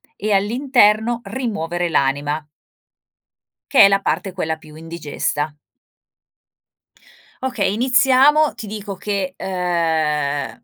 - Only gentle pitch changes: No, wide, 5.8 semitones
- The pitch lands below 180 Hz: No, high, 190 Hz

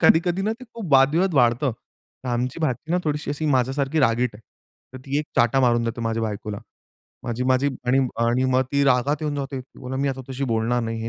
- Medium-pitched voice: No, low, 130 Hz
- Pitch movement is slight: No, average, 3.4 semitones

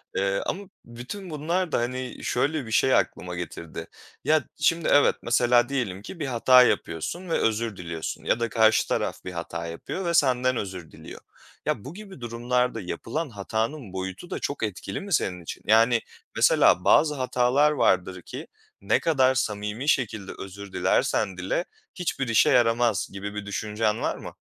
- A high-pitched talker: No, low, 115 Hz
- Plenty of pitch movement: Yes, wide, 5.9 semitones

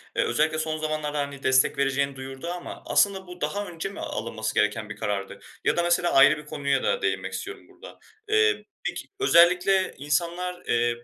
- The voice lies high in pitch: No, medium, 155 Hz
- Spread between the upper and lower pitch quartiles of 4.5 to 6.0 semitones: Yes, average, 5.1 semitones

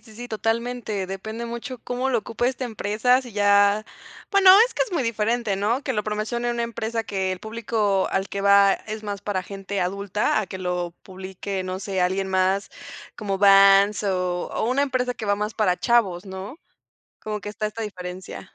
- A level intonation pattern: No, average, 3.2 semitones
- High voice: Yes, high, 210 Hz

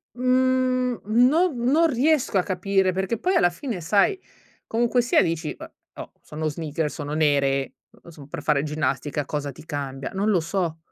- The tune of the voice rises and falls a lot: Yes, wide, 8.5 semitones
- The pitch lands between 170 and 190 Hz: Yes, medium, 185 Hz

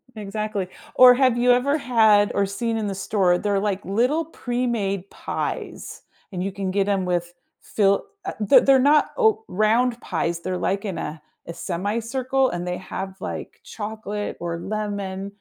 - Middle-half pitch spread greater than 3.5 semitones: Yes, average, 4.0 semitones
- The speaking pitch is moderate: No, high, 205 Hz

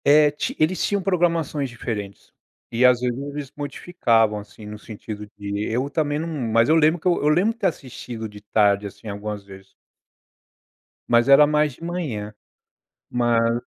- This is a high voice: No, low, 125 Hz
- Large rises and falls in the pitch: Yes, wide, 6.1 semitones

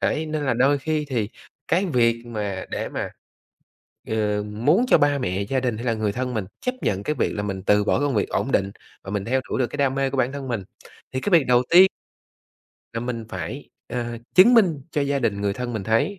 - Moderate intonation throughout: Yes, average, 4.8 semitones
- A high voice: No, low, 125 Hz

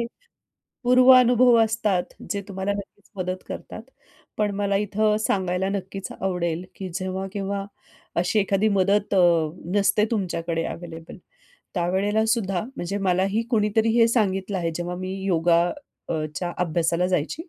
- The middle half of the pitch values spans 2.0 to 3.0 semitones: Yes, narrow, 2.6 semitones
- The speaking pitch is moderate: No, high, 195 Hz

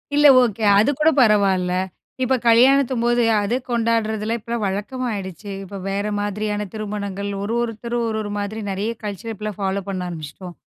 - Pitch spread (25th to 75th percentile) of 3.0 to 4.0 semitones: No, narrow, 2.6 semitones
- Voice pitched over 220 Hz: No, high, 210 Hz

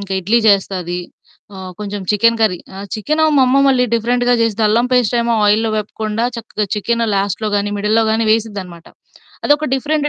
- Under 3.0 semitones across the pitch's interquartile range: Yes, narrow, 2.5 semitones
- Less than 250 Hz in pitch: Yes, high, 220 Hz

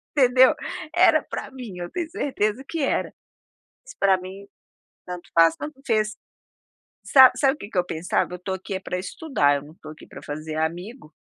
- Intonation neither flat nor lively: No, wide, 7.2 semitones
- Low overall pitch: No, high, 195 Hz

